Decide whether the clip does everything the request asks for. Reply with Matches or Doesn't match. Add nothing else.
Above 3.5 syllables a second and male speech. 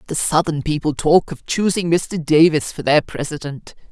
Doesn't match